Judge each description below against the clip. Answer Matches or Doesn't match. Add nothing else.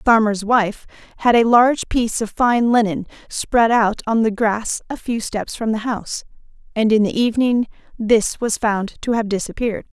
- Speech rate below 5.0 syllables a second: Doesn't match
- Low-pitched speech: Doesn't match